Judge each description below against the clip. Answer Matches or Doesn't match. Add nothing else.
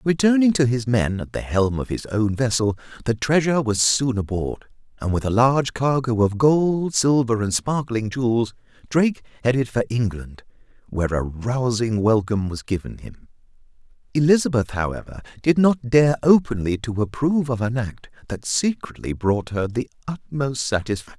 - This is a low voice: Matches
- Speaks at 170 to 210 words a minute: Doesn't match